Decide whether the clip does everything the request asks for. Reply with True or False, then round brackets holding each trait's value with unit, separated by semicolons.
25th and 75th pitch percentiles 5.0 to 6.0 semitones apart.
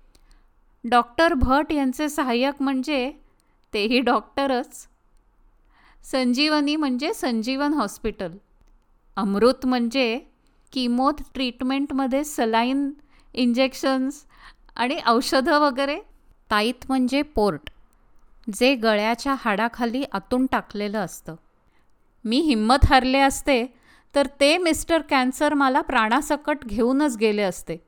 False (3.4 semitones)